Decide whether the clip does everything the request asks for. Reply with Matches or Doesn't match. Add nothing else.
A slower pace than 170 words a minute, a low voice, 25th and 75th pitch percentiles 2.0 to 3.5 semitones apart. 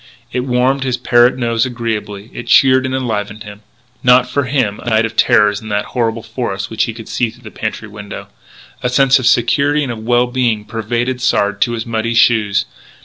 Doesn't match